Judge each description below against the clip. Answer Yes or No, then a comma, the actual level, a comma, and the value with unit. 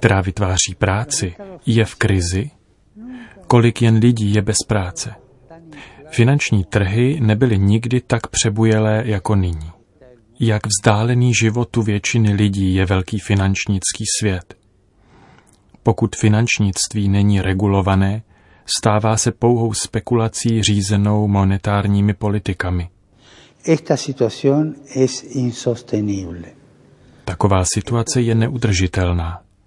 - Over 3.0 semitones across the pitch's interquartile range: Yes, average, 3.4 semitones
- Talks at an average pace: No, slow, 90 wpm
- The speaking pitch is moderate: No, low, 110 Hz